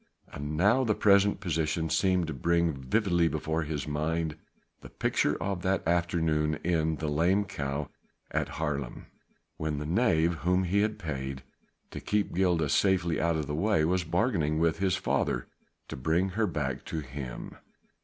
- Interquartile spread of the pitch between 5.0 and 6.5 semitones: No, average, 3.5 semitones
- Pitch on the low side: Yes, very low, 80 Hz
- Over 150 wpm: Yes, average, 165 wpm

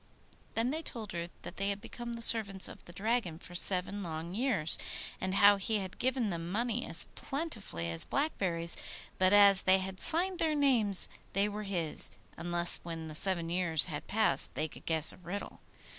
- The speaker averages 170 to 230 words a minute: Yes, average, 190 wpm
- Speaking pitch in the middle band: No, high, 195 Hz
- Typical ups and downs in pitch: Yes, average, 4.8 semitones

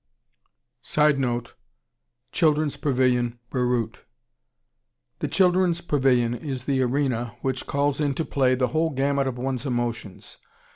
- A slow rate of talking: Yes, slow, 110 wpm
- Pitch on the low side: Yes, low, 130 Hz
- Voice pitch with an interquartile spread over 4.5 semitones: No, average, 2.9 semitones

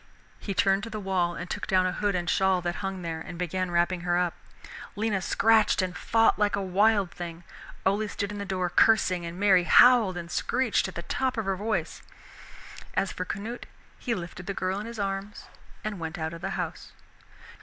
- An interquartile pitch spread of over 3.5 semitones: No, average, 2.7 semitones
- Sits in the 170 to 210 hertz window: Yes, high, 190 Hz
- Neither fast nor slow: No, fast, 210 wpm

